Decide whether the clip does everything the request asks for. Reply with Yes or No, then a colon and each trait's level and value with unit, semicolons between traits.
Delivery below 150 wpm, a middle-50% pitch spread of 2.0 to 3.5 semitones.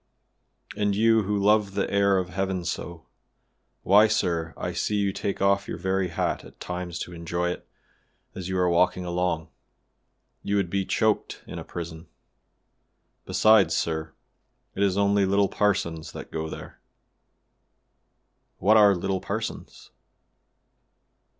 Yes: average, 140 wpm; narrow, 2.5 semitones